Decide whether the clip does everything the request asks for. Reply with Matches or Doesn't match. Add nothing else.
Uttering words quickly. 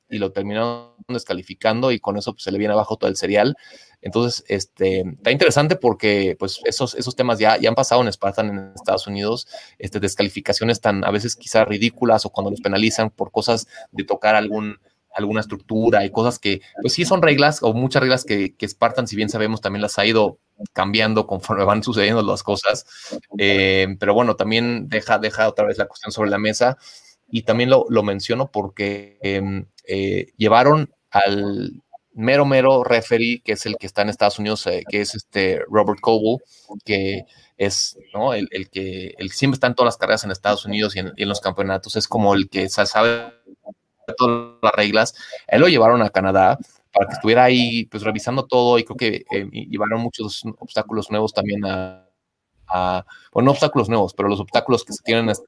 Matches